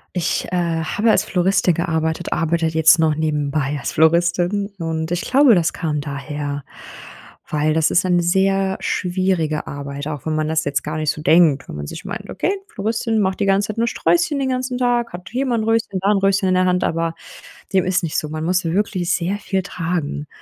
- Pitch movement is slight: No, average, 3.9 semitones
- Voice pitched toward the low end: No, medium, 175 Hz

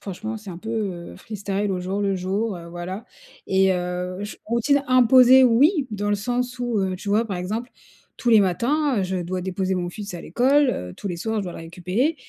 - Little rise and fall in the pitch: No, average, 4.7 semitones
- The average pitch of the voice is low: No, high, 205 Hz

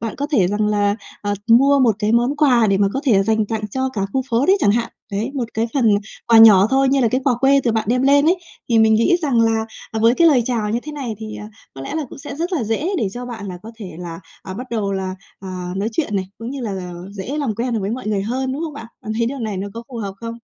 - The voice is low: No, high, 230 Hz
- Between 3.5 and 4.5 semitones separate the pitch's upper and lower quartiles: Yes, average, 4.2 semitones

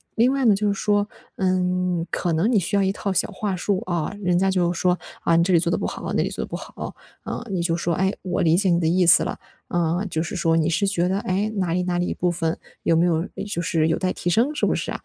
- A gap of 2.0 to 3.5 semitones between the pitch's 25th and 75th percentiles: Yes, narrow, 2.4 semitones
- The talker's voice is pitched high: No, medium, 180 Hz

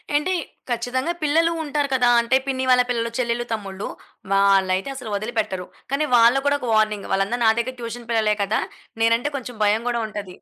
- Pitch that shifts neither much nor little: Yes, average, 3.4 semitones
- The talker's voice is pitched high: Yes, high, 235 Hz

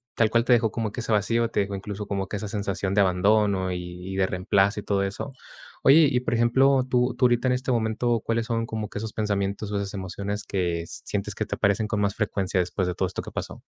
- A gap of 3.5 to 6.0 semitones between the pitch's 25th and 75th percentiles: No, average, 2.9 semitones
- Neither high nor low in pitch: No, low, 105 Hz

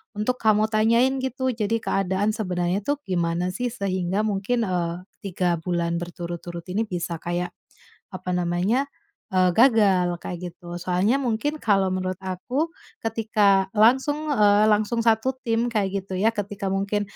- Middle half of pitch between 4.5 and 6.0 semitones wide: No, average, 3.9 semitones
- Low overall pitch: No, high, 200 Hz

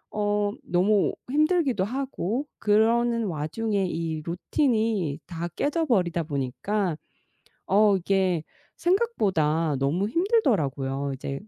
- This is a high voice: Yes, high, 200 Hz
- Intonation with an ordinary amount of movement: No, wide, 6.3 semitones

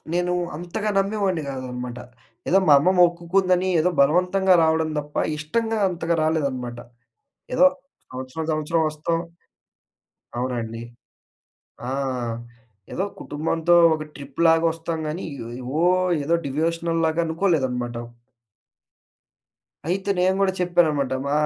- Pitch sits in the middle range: Yes, medium, 165 Hz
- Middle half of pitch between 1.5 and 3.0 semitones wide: No, average, 3.7 semitones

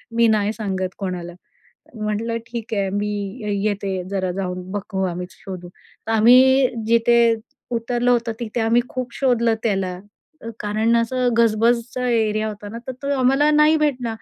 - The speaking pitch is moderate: No, high, 225 Hz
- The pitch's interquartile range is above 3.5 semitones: No, average, 3.1 semitones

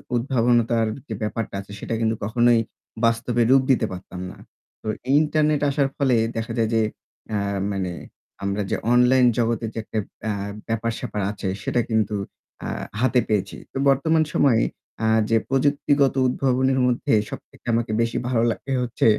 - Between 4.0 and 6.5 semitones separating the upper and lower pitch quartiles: No, average, 2.9 semitones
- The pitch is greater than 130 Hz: No, low, 120 Hz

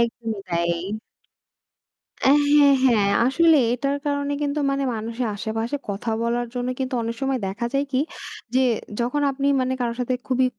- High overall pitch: Yes, very high, 255 Hz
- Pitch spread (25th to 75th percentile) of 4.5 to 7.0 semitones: No, average, 3.2 semitones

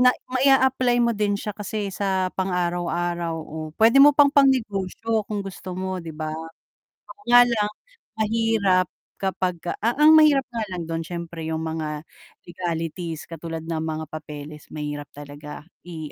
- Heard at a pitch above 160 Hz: Yes, medium, 185 Hz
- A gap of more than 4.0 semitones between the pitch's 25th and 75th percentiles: Yes, wide, 5.5 semitones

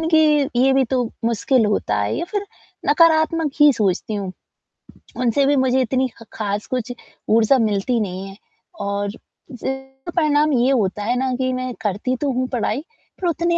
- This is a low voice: No, very high, 255 Hz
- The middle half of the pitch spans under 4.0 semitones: No, wide, 5.4 semitones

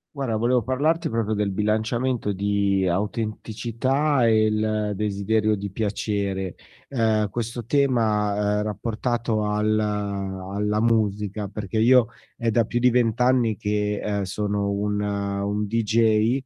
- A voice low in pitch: Yes, low, 105 Hz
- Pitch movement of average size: No, narrow, 2.2 semitones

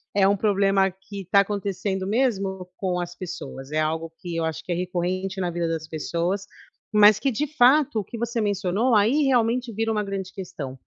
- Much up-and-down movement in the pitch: No, average, 3.4 semitones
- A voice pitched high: Yes, high, 195 Hz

